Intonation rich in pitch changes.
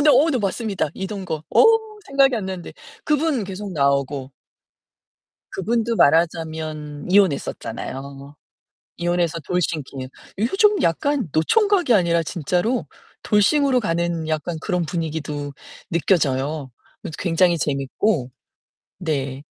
Yes: wide, 5.9 semitones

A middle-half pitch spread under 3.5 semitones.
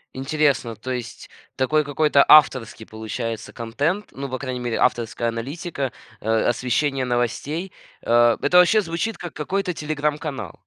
No: average, 4.4 semitones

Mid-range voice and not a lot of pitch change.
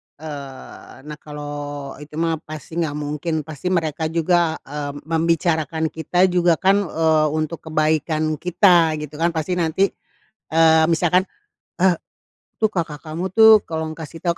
Yes: medium, 160 Hz; narrow, 2.0 semitones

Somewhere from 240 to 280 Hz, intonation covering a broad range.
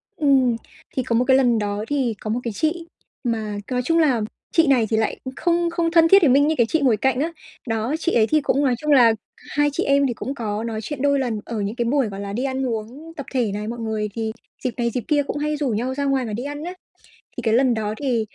No: very high, 255 Hz; average, 4.3 semitones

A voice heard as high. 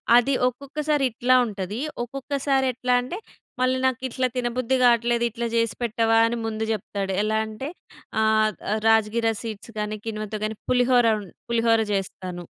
Yes: high, 230 Hz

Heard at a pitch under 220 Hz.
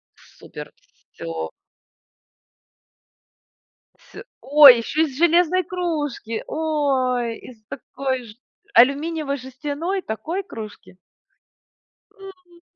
No: very high, 285 Hz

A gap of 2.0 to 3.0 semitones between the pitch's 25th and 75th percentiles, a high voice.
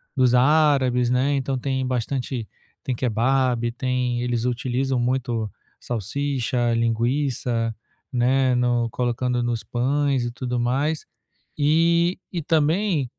No: narrow, 2.4 semitones; low, 125 Hz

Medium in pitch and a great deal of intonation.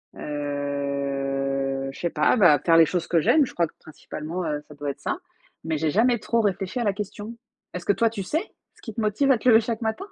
Yes: medium, 170 Hz; wide, 7.2 semitones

